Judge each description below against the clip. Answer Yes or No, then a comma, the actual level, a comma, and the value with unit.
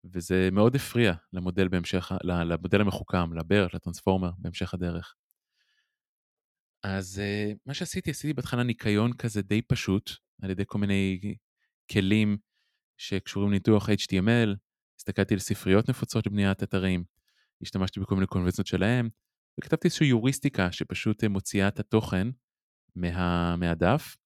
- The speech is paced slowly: No, average, 115 wpm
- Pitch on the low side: Yes, low, 100 Hz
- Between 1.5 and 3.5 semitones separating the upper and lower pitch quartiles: Yes, average, 2.9 semitones